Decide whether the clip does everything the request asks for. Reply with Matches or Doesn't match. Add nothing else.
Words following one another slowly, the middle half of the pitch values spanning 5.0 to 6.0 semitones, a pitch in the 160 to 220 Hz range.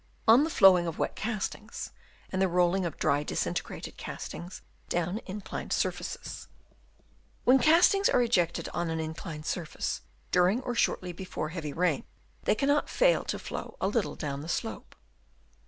Doesn't match